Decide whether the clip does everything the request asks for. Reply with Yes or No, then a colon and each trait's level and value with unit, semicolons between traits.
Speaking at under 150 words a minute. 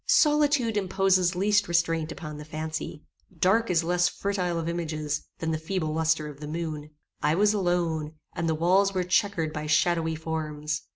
No: average, 170 wpm